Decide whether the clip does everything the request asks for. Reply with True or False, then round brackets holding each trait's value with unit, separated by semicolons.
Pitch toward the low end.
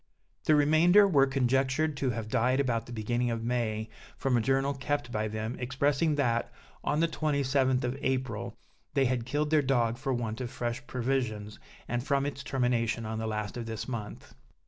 True (125 Hz)